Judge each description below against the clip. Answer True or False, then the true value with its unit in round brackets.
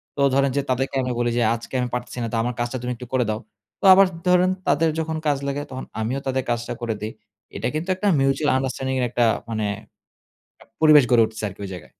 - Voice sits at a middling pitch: False (130 Hz)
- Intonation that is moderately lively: True (3.2 semitones)